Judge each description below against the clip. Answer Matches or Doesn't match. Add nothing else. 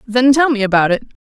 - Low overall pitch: Doesn't match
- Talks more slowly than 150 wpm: Doesn't match